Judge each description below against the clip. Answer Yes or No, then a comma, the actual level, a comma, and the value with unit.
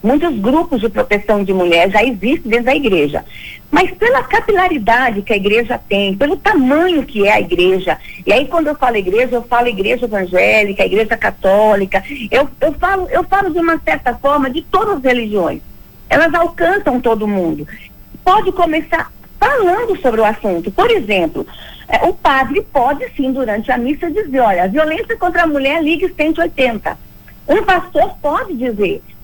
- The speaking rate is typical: Yes, average, 165 wpm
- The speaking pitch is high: Yes, very high, 275 Hz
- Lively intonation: Yes, wide, 7.6 semitones